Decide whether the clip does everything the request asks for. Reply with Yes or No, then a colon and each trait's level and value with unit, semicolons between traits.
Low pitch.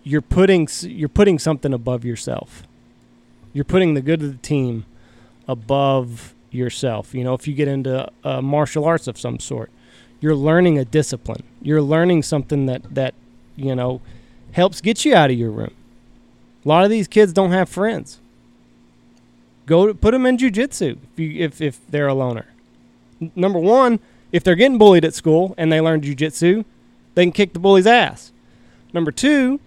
No: medium, 145 Hz